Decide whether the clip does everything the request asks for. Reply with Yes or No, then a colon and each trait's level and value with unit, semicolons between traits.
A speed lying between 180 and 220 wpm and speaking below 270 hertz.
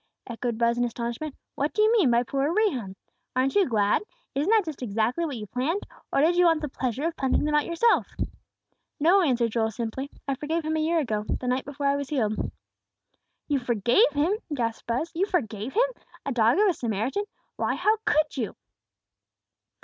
No: average, 195 wpm; very high, 275 Hz